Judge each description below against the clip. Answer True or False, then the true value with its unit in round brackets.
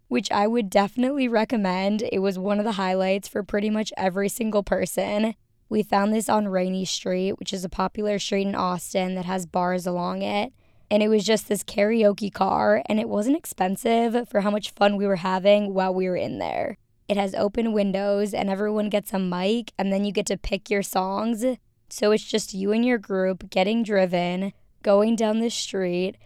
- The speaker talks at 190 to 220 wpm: True (200 wpm)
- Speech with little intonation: True (2.1 semitones)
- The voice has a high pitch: True (200 Hz)